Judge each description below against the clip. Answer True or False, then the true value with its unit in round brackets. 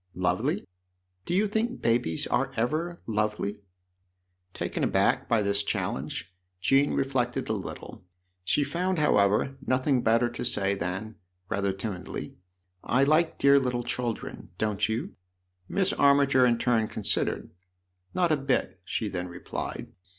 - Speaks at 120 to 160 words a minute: True (150 wpm)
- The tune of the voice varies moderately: False (5.8 semitones)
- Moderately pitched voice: False (120 Hz)